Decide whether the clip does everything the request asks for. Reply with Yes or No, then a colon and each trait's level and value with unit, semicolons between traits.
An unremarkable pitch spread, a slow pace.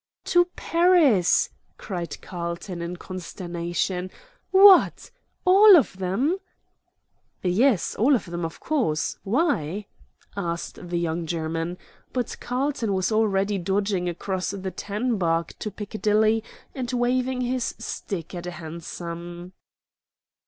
No: wide, 6.1 semitones; slow, 115 wpm